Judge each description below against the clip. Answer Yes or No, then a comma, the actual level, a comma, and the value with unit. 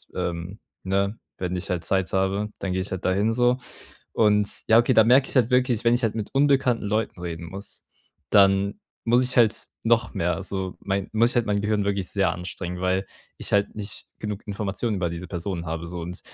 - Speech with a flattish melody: No, average, 3.4 semitones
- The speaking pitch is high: No, low, 100 Hz